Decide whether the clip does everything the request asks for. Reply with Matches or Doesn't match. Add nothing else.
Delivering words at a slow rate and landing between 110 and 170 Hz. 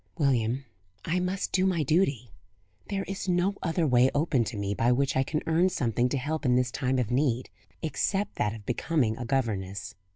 Doesn't match